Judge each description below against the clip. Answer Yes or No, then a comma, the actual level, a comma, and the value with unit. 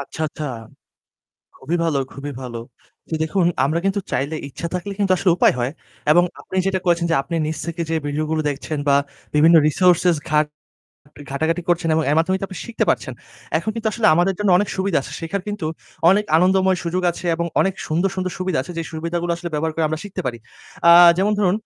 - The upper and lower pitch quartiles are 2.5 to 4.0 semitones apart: Yes, average, 3.2 semitones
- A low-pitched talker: No, medium, 170 Hz